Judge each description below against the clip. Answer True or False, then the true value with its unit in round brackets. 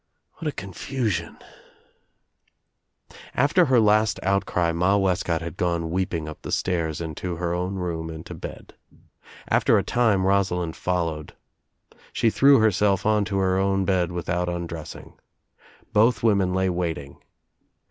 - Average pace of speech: True (145 wpm)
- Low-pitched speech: True (90 Hz)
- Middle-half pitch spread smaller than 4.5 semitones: True (3.1 semitones)